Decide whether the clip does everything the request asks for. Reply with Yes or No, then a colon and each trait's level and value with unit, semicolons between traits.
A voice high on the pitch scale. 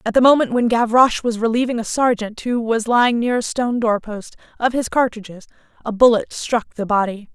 Yes: high, 230 Hz